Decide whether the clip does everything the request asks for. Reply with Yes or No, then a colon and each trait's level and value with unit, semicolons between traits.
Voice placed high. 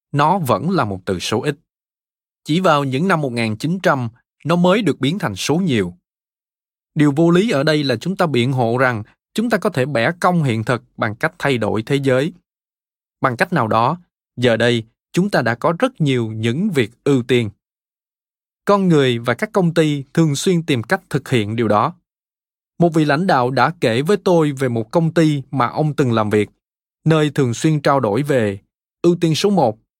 No: medium, 140 Hz